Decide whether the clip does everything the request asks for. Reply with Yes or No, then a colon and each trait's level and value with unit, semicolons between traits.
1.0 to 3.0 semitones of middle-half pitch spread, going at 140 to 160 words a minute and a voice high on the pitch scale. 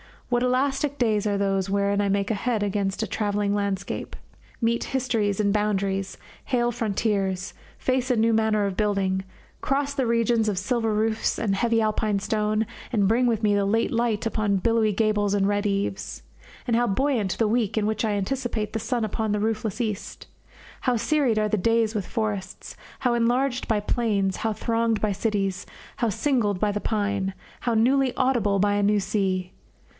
No: narrow, 2.5 semitones; average, 180 wpm; high, 215 Hz